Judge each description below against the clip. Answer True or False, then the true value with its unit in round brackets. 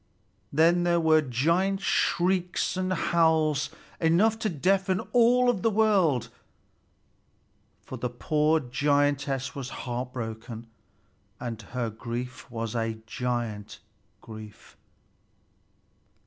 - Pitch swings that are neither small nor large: False (6.6 semitones)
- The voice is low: False (145 Hz)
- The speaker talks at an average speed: False (95 wpm)